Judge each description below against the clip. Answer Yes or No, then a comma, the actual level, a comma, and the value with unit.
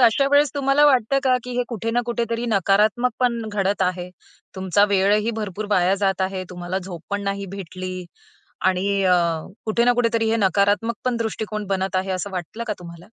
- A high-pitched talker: Yes, high, 205 Hz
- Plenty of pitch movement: No, average, 3.7 semitones